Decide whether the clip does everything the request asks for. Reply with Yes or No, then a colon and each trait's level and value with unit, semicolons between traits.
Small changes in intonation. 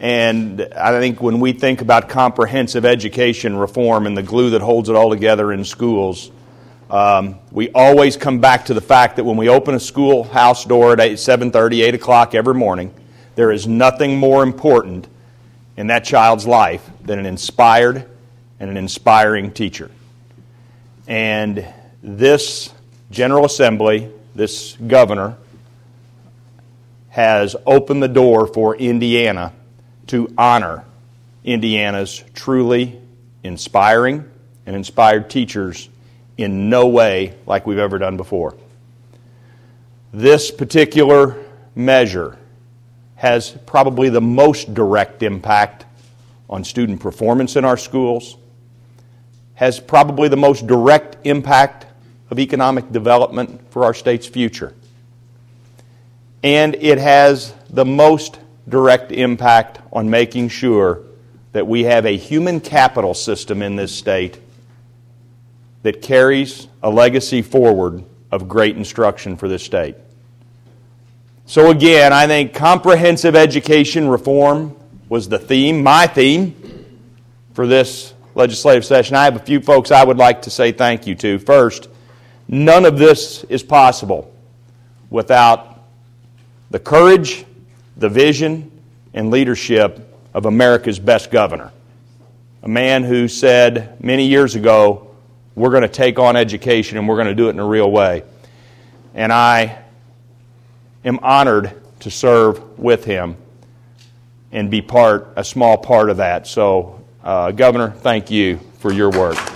Yes: narrow, 2.2 semitones